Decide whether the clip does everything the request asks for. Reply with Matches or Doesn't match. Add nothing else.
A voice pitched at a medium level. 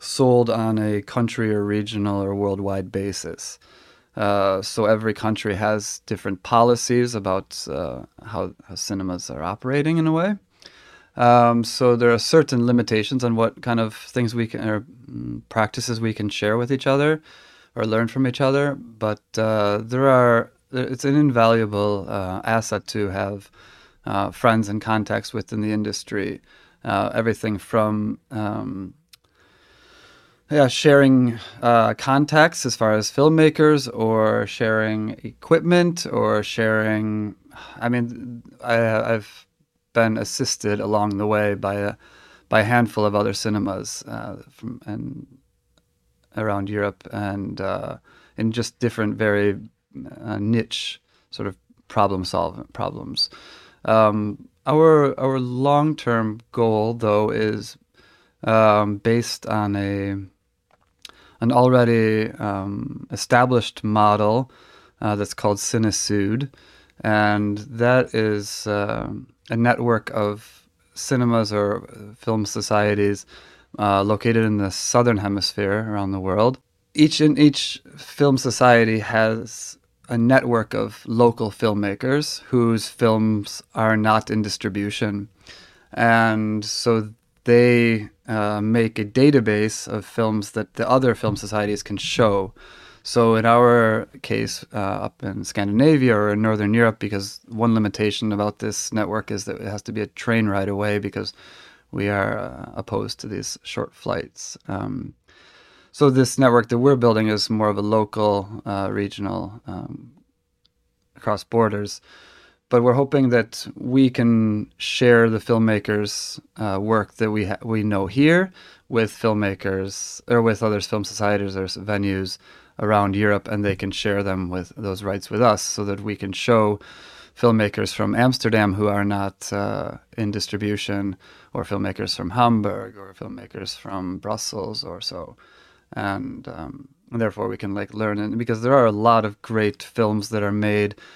Doesn't match